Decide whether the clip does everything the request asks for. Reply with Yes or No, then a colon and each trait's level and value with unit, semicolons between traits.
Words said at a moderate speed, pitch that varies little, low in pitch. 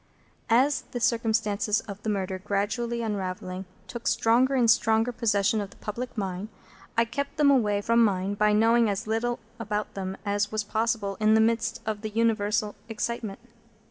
No: average, 170 wpm; narrow, 2.2 semitones; high, 220 Hz